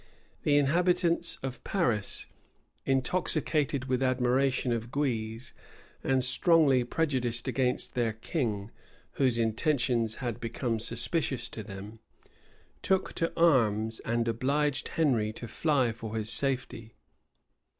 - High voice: No, low, 125 Hz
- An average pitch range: Yes, average, 4.0 semitones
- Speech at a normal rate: No, slow, 110 wpm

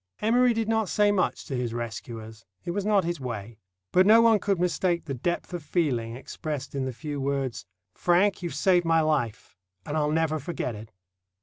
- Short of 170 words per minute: No, average, 195 wpm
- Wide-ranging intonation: Yes, wide, 6.7 semitones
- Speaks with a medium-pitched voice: Yes, medium, 155 Hz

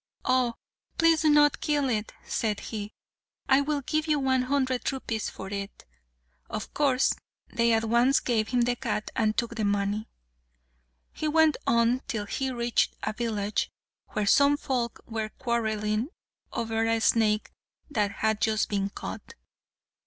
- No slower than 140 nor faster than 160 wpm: Yes, average, 150 wpm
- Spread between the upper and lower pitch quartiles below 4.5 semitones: Yes, average, 3.7 semitones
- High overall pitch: Yes, high, 235 Hz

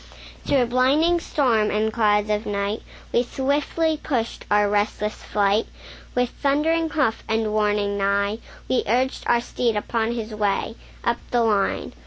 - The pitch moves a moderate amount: Yes, average, 3.7 semitones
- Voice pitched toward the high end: Yes, high, 225 Hz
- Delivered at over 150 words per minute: No, average, 145 wpm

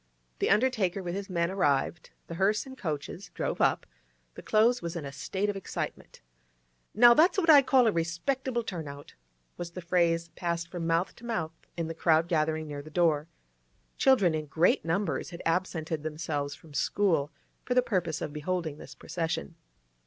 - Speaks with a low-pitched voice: No, medium, 170 Hz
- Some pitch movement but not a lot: Yes, average, 4.2 semitones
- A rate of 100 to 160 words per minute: No, average, 180 wpm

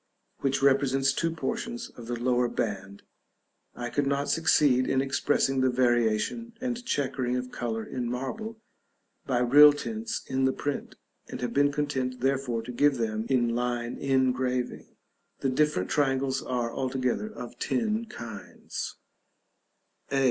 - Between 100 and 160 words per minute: Yes, average, 140 wpm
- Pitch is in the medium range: No, low, 130 Hz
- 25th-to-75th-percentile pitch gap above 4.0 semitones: No, average, 2.7 semitones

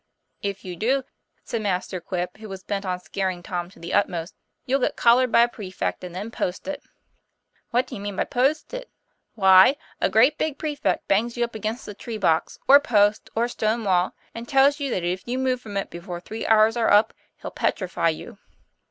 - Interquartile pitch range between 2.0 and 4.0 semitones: No, average, 4.7 semitones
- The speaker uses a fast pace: Yes, fast, 215 wpm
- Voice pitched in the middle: No, high, 215 Hz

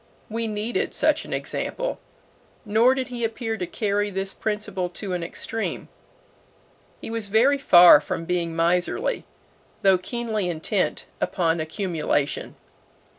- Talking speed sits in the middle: No, slow, 125 wpm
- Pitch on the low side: No, high, 205 Hz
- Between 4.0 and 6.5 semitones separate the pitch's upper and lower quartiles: Yes, average, 4.3 semitones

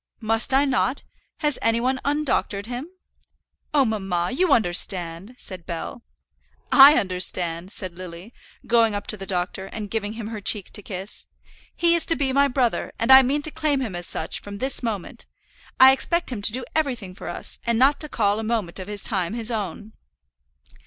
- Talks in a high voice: Yes, high, 225 Hz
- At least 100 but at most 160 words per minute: No, average, 190 wpm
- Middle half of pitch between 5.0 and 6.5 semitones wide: Yes, wide, 5.4 semitones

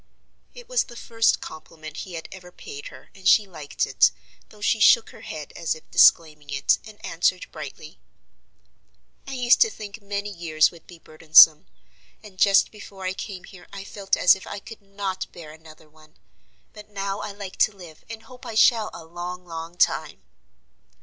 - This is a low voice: No, medium, 185 Hz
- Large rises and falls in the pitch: No, average, 4.2 semitones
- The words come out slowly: No, average, 185 wpm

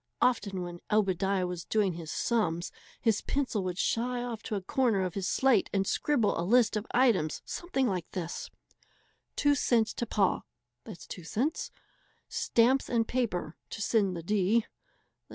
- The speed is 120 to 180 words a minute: Yes, average, 155 wpm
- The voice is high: Yes, high, 210 Hz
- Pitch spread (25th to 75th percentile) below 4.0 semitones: No, average, 4.8 semitones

